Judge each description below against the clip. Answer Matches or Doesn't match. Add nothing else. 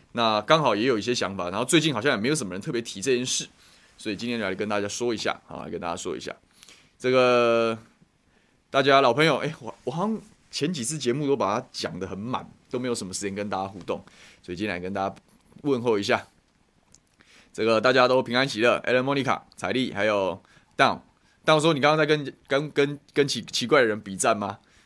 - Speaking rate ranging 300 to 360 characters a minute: Matches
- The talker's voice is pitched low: Matches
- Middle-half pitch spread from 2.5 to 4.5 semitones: Doesn't match